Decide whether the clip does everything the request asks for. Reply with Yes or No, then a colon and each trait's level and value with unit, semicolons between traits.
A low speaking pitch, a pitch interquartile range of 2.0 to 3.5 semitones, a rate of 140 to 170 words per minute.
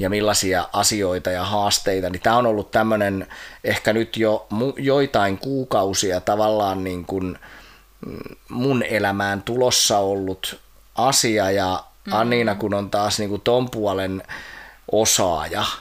No: low, 105 Hz; narrow, 2.4 semitones; average, 130 wpm